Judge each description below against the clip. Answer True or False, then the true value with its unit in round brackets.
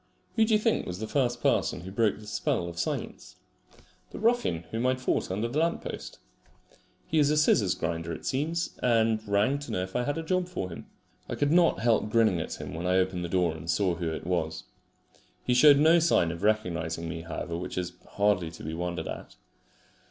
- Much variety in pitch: True (8.5 semitones)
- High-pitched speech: False (105 Hz)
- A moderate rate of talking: False (220 wpm)